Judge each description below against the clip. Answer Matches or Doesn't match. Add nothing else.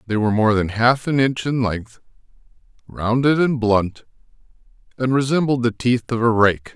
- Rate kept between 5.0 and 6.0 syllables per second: Doesn't match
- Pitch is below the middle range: Matches